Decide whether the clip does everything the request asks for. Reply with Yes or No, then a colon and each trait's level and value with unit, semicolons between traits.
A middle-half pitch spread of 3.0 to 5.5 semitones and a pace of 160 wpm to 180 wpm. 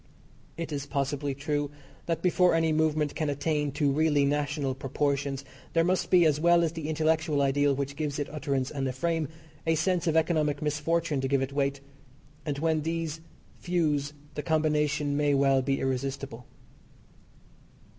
No: narrow, 2.4 semitones; average, 165 wpm